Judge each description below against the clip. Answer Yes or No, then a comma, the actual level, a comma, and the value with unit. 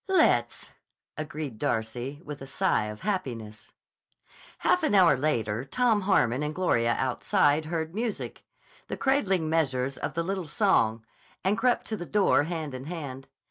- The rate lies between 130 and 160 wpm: Yes, average, 150 wpm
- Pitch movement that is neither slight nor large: No, wide, 6.8 semitones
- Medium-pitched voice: Yes, medium, 155 Hz